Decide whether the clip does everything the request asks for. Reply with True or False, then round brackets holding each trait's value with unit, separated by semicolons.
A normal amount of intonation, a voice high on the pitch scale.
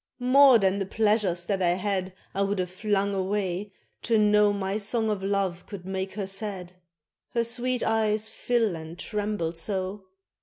False (2.1 semitones; 200 Hz)